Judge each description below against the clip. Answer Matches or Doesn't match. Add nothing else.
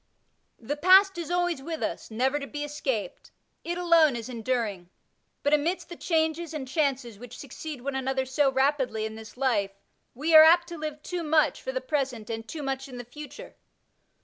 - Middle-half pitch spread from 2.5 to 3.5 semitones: Doesn't match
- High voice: Matches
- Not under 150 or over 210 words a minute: Matches